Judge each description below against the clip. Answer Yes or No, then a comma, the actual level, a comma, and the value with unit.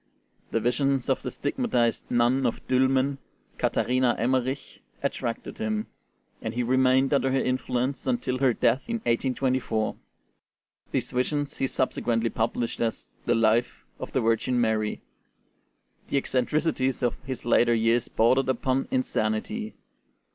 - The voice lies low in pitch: Yes, low, 130 Hz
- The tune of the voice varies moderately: No, narrow, 2.3 semitones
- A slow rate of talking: Yes, slow, 130 wpm